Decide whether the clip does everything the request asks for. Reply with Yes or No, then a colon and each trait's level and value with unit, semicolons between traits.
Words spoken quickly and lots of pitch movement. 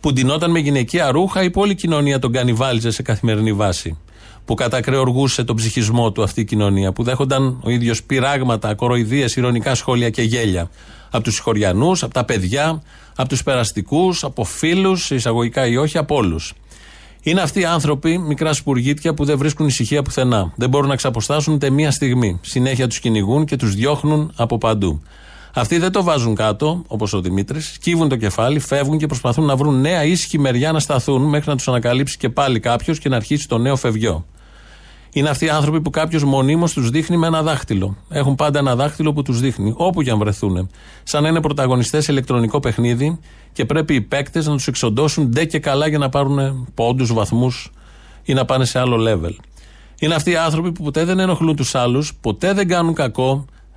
No: fast, 190 wpm; average, 4.7 semitones